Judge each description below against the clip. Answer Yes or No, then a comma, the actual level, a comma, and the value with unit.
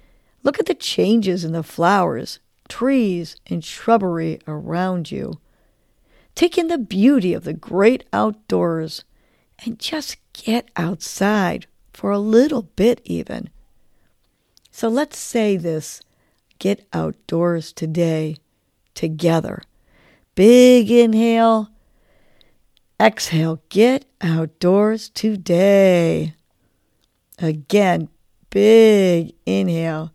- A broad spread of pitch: Yes, wide, 5.8 semitones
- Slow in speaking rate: Yes, slow, 90 wpm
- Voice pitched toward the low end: No, medium, 185 Hz